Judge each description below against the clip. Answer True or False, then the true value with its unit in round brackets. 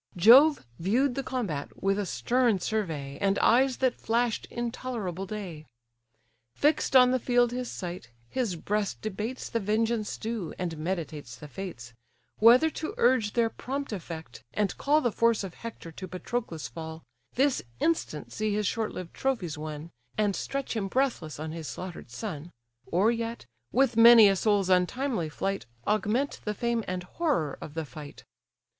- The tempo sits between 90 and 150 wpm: False (160 wpm)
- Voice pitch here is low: False (210 Hz)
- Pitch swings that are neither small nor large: False (5.8 semitones)